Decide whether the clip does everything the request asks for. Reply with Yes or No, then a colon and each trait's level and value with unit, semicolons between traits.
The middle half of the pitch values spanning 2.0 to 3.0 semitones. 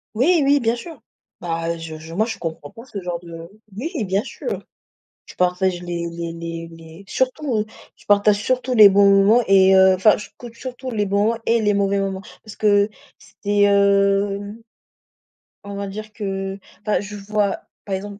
Yes: narrow, 2.4 semitones